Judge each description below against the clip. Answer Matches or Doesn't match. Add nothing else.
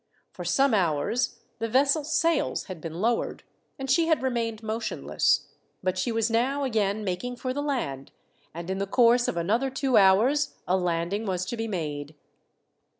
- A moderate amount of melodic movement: Doesn't match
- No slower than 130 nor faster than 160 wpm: Doesn't match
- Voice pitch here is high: Matches